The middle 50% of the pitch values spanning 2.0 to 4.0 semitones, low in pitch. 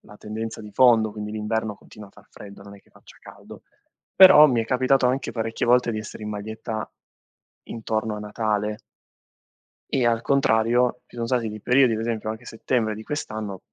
Yes: narrow, 2.4 semitones; low, 110 Hz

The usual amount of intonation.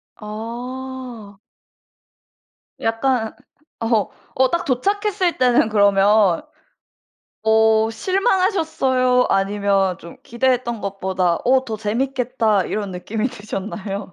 Yes: average, 4.1 semitones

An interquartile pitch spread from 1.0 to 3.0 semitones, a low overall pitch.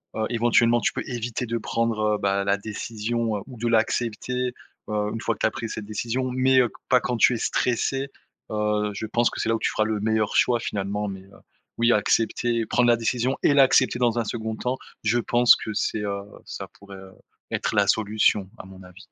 Yes: narrow, 2.4 semitones; low, 115 Hz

